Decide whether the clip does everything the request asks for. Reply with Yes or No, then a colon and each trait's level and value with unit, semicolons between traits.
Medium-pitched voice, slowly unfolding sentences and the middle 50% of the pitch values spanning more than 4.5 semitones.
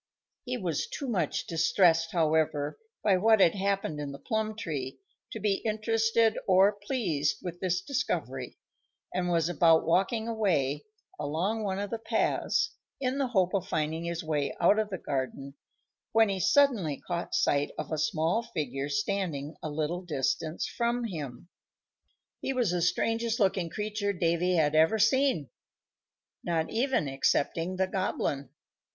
No: medium, 180 Hz; average, 150 wpm; wide, 5.6 semitones